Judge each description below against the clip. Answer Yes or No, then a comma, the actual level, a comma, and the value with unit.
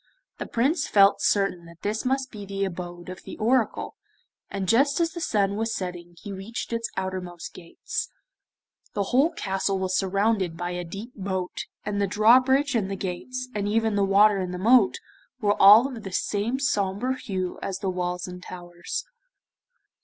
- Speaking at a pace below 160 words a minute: No, average, 175 wpm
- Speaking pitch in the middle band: No, high, 200 Hz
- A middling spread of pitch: Yes, average, 3.8 semitones